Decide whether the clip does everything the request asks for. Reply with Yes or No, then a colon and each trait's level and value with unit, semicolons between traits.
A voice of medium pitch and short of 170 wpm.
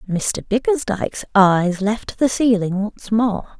No: high, 215 Hz; slow, 135 wpm